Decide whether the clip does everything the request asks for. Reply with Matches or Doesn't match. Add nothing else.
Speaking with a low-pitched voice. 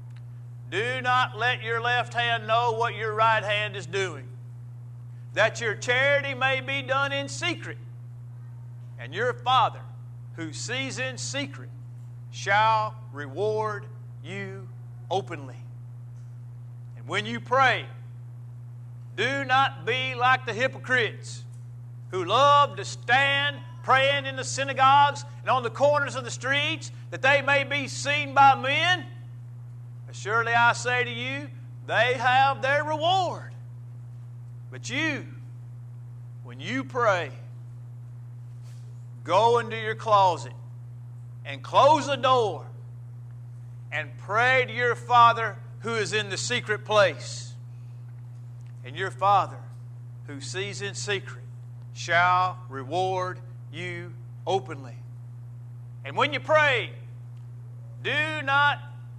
Matches